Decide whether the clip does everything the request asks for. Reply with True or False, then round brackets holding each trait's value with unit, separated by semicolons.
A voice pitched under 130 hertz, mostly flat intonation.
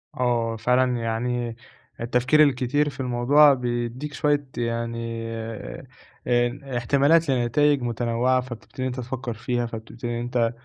True (120 Hz; 2.0 semitones)